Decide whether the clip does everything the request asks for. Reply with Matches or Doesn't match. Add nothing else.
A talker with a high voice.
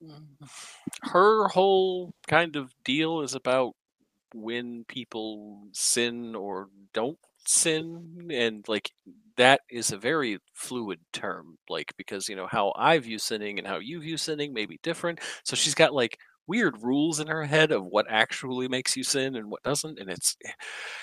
Doesn't match